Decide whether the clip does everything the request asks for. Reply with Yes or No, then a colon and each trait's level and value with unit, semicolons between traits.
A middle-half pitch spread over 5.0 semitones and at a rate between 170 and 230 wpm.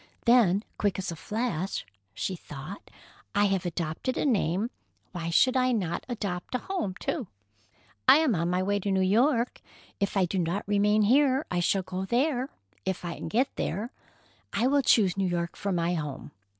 Yes: wide, 5.4 semitones; average, 175 wpm